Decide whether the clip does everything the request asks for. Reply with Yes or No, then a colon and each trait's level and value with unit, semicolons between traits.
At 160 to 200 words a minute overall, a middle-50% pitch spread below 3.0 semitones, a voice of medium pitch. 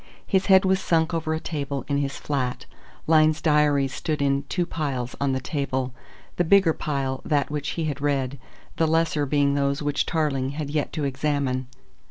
Yes: average, 185 wpm; narrow, 2.4 semitones; medium, 145 Hz